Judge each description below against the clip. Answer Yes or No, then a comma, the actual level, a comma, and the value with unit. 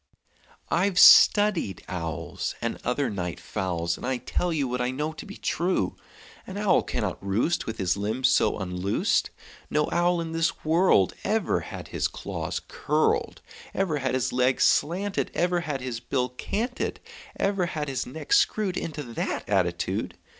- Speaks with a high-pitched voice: No, medium, 145 Hz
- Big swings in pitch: Yes, wide, 7.6 semitones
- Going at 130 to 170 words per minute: Yes, average, 160 wpm